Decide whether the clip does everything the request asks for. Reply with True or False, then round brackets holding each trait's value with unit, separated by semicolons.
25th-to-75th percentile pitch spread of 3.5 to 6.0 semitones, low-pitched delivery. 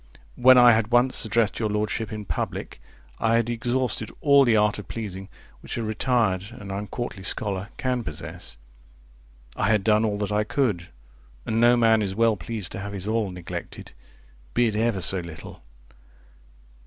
False (3.1 semitones; 110 Hz)